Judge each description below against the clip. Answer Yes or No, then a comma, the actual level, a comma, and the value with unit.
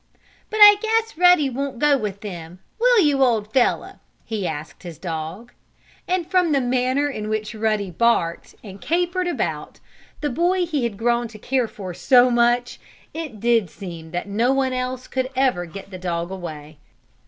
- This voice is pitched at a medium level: No, high, 240 Hz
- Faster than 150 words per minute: Yes, average, 175 wpm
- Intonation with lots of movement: Yes, wide, 6.5 semitones